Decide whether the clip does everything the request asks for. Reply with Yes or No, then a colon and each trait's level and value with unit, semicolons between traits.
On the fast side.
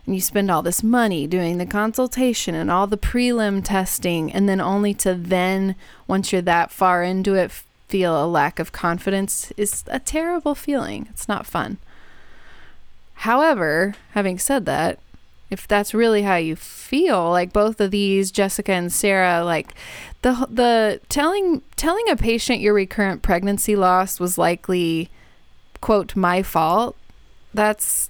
No: average, 150 wpm